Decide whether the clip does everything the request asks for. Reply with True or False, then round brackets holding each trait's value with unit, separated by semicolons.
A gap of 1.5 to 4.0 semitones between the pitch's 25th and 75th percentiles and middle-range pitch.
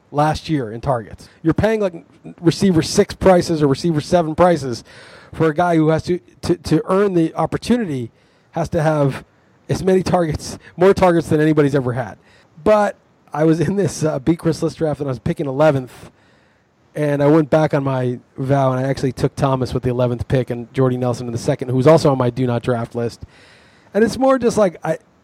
False (4.6 semitones; 155 Hz)